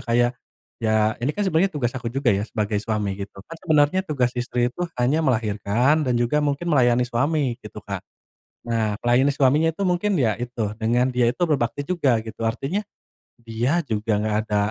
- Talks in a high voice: No, low, 125 Hz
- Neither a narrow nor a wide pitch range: Yes, average, 4.7 semitones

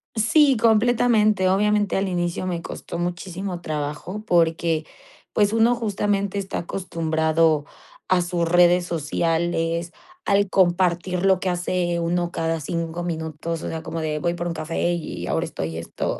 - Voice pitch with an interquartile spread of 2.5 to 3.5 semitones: Yes, average, 2.8 semitones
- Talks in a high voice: No, medium, 175 Hz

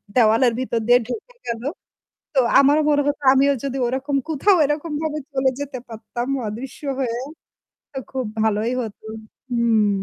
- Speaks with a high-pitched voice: Yes, very high, 260 Hz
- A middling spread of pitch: Yes, average, 3.7 semitones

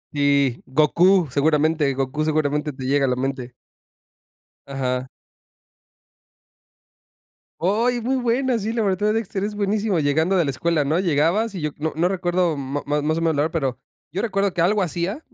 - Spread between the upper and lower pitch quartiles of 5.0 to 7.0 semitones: Yes, wide, 5.6 semitones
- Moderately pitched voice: Yes, medium, 160 Hz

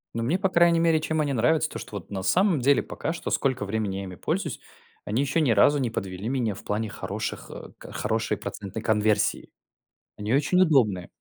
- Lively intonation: Yes, wide, 7.0 semitones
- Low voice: Yes, low, 120 Hz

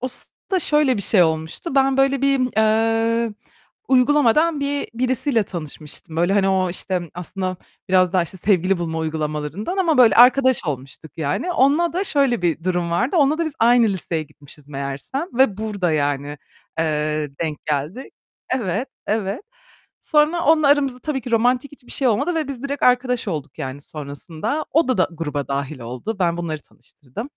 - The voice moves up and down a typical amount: No, wide, 8.8 semitones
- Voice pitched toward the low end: No, high, 210 Hz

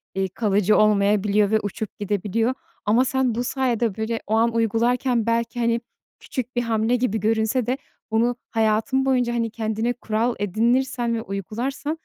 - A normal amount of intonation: No, narrow, 2.2 semitones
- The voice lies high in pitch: Yes, high, 230 Hz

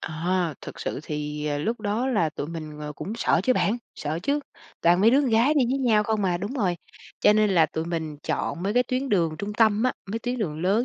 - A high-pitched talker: Yes, high, 200 Hz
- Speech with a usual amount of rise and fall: No, wide, 6.2 semitones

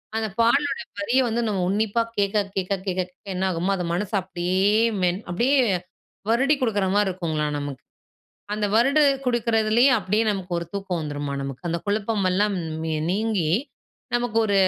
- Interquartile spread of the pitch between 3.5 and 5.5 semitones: Yes, average, 4.0 semitones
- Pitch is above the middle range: Yes, high, 200 Hz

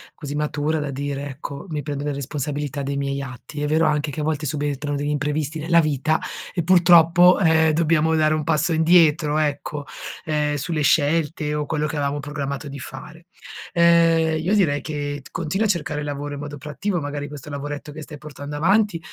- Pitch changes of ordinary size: No, narrow, 1.9 semitones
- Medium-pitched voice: Yes, medium, 150 Hz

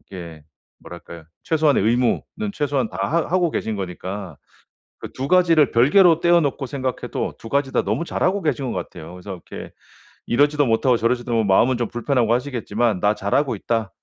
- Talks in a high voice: No, low, 120 Hz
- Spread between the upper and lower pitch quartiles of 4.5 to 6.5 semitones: Yes, wide, 6.0 semitones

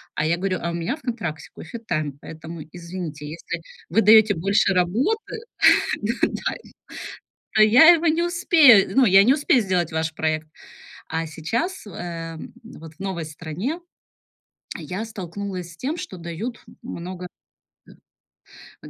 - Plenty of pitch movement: Yes, wide, 5.9 semitones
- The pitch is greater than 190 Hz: No, medium, 185 Hz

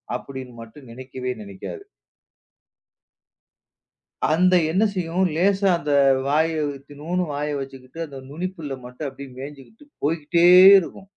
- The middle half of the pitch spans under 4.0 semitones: No, average, 4.7 semitones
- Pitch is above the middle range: No, medium, 150 Hz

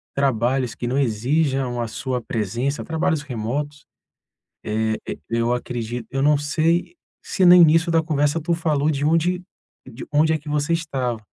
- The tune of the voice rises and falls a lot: No, average, 4.5 semitones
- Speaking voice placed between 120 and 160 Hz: Yes, medium, 140 Hz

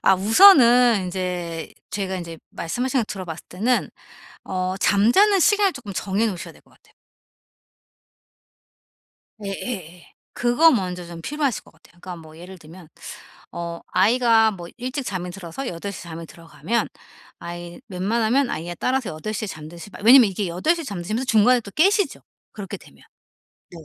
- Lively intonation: Yes, wide, 5.8 semitones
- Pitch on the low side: No, high, 195 Hz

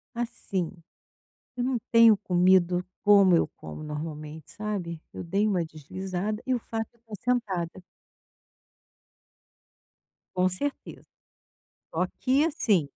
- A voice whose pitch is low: No, high, 190 Hz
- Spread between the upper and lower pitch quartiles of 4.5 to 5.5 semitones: Yes, average, 4.9 semitones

